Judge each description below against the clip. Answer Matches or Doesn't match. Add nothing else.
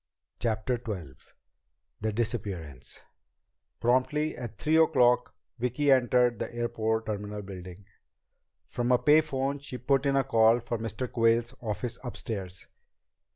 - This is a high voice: Doesn't match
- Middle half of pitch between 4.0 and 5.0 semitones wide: Doesn't match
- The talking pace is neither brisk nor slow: Doesn't match